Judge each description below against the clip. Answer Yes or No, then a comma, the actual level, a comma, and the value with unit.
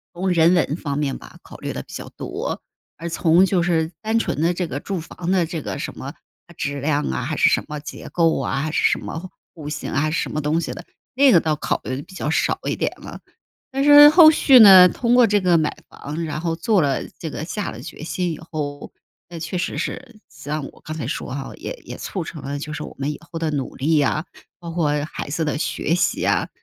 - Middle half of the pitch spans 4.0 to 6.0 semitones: No, average, 3.3 semitones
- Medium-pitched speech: Yes, medium, 160 Hz